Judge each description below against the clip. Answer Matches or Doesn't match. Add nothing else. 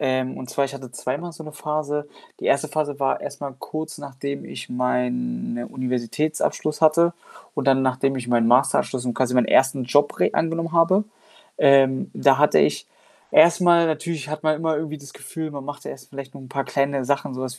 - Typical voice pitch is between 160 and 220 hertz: Doesn't match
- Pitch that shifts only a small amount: Doesn't match